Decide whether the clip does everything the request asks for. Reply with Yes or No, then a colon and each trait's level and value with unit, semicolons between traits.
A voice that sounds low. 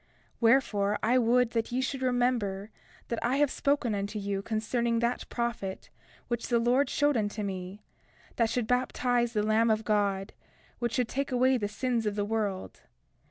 No: high, 230 Hz